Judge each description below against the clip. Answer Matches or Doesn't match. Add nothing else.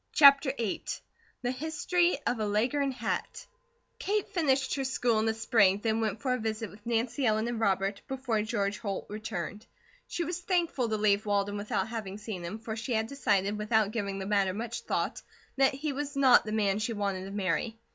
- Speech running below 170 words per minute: Doesn't match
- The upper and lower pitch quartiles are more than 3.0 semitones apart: Matches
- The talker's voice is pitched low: Doesn't match